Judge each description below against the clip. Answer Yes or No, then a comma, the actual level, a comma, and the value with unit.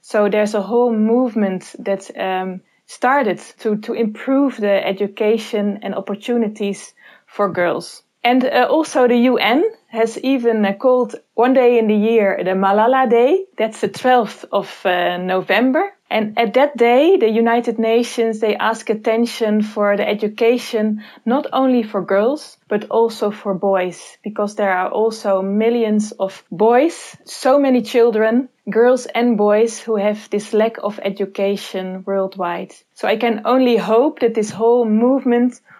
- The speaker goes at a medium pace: Yes, average, 150 wpm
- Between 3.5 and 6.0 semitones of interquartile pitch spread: No, average, 2.9 semitones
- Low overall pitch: No, high, 225 Hz